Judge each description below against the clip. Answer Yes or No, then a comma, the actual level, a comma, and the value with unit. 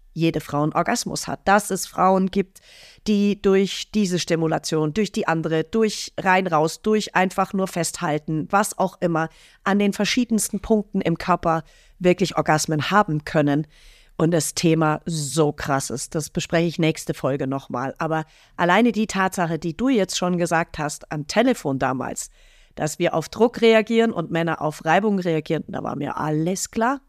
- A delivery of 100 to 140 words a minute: No, average, 165 wpm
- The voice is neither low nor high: Yes, medium, 170 Hz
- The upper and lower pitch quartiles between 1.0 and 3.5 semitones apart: No, average, 4.0 semitones